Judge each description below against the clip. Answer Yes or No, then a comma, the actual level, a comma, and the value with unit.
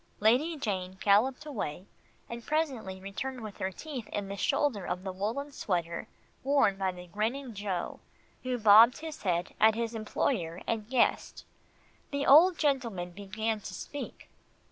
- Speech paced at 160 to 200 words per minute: No, average, 150 wpm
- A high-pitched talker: Yes, high, 220 Hz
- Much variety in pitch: Yes, wide, 5.7 semitones